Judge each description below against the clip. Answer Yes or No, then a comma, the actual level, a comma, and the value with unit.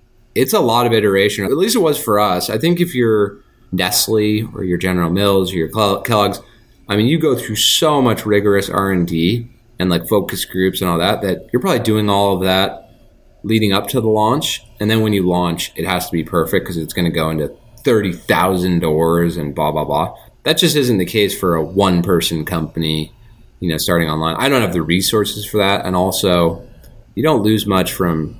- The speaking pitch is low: Yes, very low, 95 Hz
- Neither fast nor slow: No, fast, 215 wpm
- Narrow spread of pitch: No, average, 4.1 semitones